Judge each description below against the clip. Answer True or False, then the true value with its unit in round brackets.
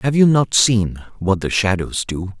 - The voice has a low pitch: True (110 Hz)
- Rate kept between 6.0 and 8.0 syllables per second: False (4.1 syllables/s)